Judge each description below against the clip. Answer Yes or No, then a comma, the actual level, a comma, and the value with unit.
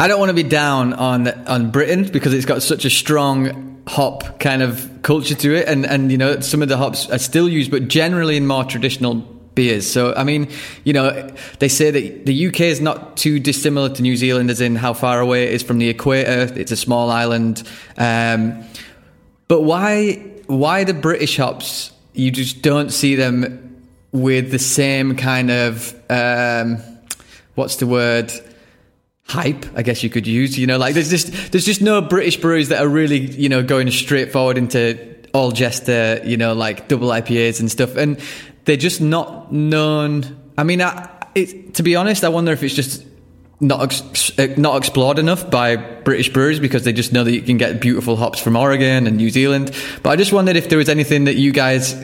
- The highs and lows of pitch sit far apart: No, average, 3.4 semitones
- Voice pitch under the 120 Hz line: No, low, 135 Hz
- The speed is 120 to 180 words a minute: No, fast, 205 wpm